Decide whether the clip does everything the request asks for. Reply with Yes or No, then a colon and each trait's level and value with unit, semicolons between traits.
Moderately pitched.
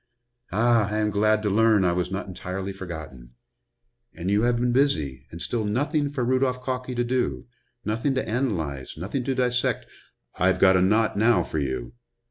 No: low, 110 Hz